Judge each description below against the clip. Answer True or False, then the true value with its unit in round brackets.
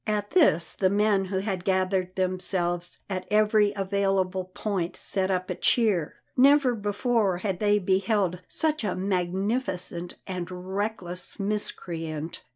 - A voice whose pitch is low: False (190 Hz)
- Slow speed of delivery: True (130 wpm)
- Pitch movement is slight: True (2.3 semitones)